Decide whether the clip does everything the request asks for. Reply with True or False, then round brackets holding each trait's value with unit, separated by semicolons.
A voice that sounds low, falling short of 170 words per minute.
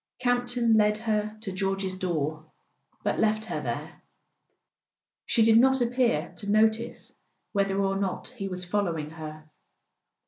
False (205 Hz; 140 wpm)